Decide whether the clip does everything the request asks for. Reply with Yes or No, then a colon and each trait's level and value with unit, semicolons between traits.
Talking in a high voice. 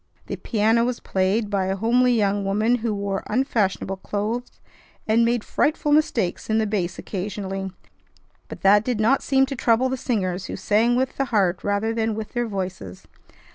Yes: high, 215 Hz